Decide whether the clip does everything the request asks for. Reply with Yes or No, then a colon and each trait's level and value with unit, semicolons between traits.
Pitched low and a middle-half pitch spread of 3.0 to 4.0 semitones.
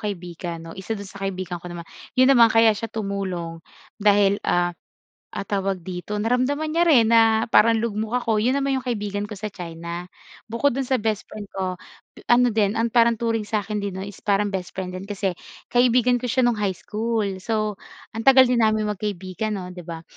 No: high, 210 Hz; average, 3.4 semitones